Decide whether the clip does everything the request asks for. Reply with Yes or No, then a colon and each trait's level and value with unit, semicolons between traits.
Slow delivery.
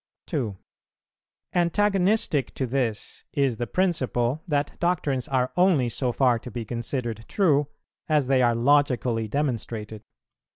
Yes: slow, 125 wpm